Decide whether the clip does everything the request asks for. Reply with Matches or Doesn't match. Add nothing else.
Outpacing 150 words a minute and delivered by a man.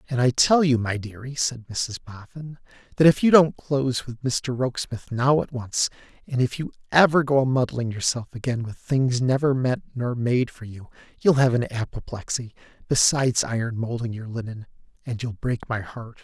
Matches